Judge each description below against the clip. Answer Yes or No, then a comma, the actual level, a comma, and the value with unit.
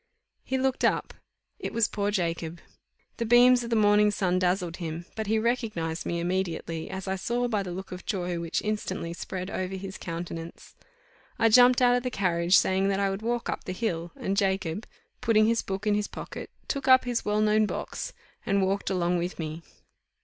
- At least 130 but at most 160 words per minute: No, average, 200 wpm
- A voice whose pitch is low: No, high, 195 Hz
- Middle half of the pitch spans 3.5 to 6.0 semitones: Yes, average, 3.9 semitones